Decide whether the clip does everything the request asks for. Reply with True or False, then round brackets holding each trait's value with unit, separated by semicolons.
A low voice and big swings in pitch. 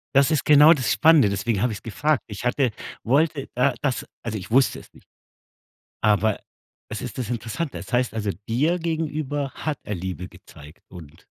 True (125 Hz; 5.9 semitones)